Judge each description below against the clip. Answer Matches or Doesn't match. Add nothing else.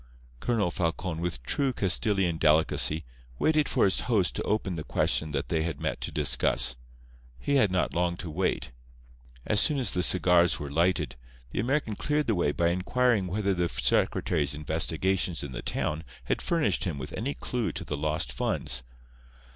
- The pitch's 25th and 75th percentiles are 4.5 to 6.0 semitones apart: Matches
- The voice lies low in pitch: Matches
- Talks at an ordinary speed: Matches